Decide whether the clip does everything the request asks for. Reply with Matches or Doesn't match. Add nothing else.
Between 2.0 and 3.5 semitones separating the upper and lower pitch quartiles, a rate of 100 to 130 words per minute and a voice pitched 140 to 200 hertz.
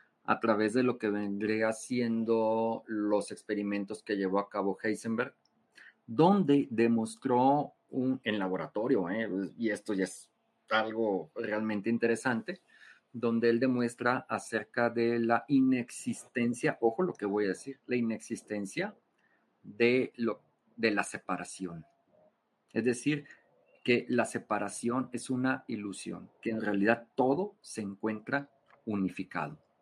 Doesn't match